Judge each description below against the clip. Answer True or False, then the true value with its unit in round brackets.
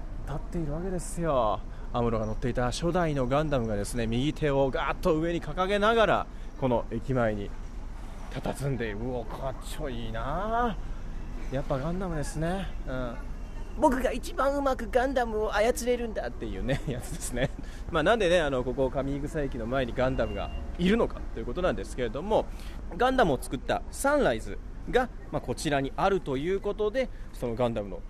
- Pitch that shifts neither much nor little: False (7.8 semitones)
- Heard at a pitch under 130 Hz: False (135 Hz)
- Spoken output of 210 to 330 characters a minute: False (380 characters per minute)